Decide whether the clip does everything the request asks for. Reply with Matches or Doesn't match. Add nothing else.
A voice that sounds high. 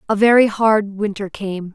Matches